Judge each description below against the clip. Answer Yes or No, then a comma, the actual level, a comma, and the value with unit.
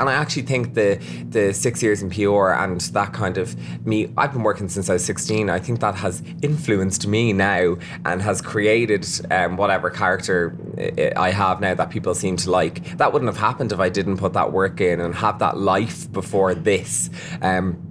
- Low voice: Yes, very low, 95 Hz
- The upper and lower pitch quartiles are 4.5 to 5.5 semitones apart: No, average, 2.9 semitones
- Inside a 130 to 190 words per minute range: No, average, 200 wpm